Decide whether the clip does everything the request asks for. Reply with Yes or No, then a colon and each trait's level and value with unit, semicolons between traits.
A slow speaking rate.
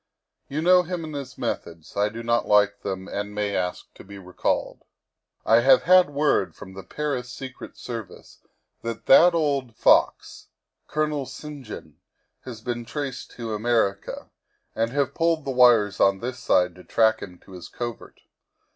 No: average, 170 wpm